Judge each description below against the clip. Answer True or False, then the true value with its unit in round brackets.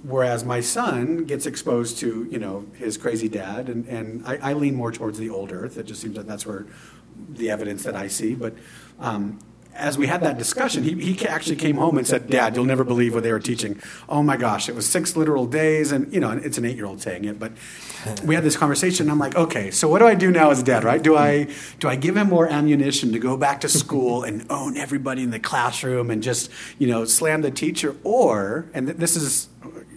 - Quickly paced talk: True (240 wpm)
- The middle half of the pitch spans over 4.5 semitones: True (4.9 semitones)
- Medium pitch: False (130 Hz)